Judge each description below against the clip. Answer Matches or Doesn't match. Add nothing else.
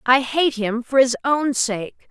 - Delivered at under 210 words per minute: Matches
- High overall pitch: Matches